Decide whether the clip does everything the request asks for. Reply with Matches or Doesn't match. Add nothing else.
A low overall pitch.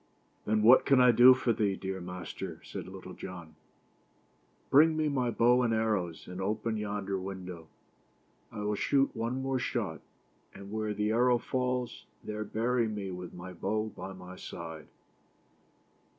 Matches